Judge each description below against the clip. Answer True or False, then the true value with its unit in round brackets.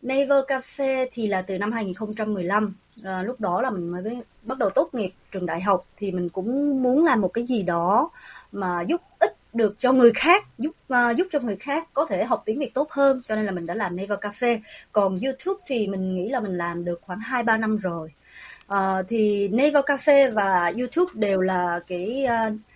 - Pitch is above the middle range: True (220 Hz)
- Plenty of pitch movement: True (5.7 semitones)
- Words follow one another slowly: False (210 wpm)